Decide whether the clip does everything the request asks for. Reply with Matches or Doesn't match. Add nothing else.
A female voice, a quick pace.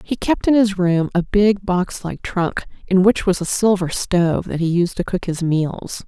Matches